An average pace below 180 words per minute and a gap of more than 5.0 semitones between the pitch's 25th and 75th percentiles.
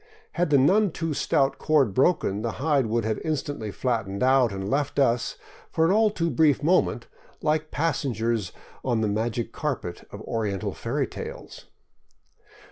Yes: average, 165 wpm; wide, 5.6 semitones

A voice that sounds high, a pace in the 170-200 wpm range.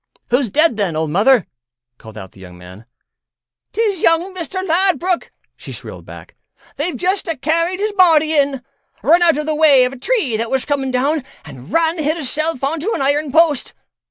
Yes: very high, 300 Hz; average, 185 wpm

